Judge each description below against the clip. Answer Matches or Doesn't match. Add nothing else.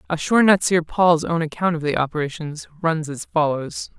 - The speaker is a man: Doesn't match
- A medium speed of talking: Matches